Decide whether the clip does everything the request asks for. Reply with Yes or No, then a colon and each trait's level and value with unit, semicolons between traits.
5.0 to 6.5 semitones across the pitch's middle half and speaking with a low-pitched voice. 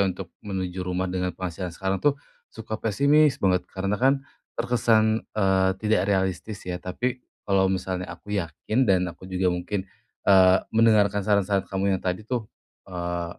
No: average, 2.9 semitones; very low, 95 Hz